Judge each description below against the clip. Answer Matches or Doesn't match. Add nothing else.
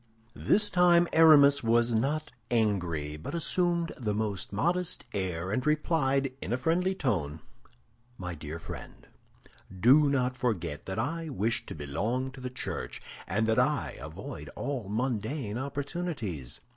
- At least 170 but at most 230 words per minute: Doesn't match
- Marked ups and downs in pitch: Matches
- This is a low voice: Matches